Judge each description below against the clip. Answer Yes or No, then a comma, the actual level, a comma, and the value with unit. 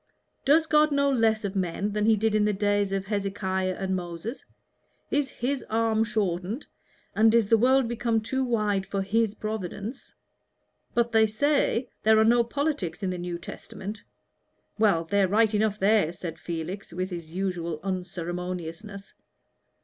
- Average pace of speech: Yes, average, 160 wpm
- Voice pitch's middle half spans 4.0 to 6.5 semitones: No, average, 3.4 semitones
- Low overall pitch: No, high, 210 Hz